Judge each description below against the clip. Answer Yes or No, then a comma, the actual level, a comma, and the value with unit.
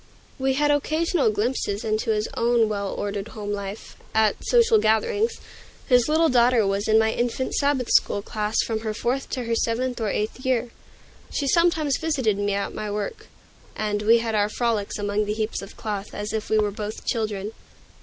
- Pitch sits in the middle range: No, high, 220 Hz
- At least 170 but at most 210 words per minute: Yes, average, 185 wpm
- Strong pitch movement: No, average, 3.6 semitones